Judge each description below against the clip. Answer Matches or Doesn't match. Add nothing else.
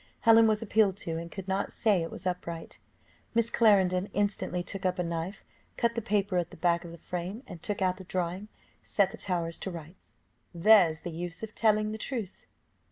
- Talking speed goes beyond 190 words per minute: Matches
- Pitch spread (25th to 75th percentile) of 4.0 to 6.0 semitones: Doesn't match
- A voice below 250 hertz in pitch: Matches